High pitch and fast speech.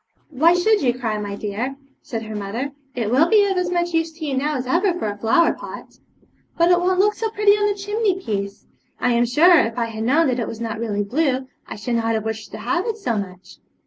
Yes: very high, 260 Hz; fast, 250 wpm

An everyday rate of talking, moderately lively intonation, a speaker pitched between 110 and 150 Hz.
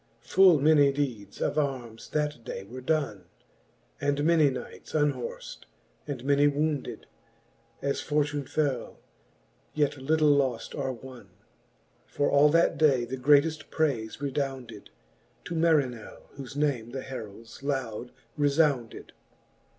No: slow, 120 wpm; average, 3.0 semitones; medium, 140 Hz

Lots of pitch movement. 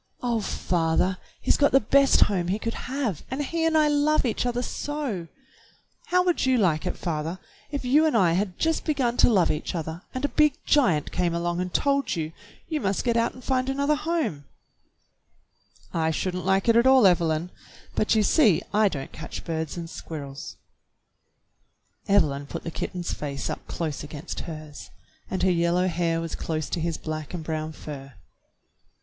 Yes: wide, 8.1 semitones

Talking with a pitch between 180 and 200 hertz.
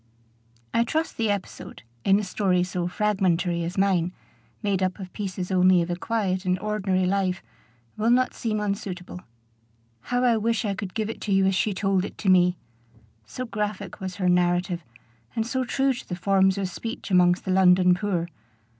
Yes: high, 190 Hz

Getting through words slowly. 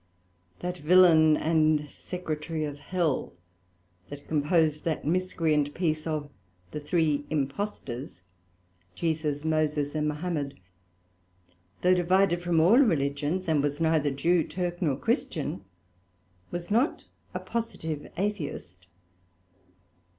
Yes: slow, 95 wpm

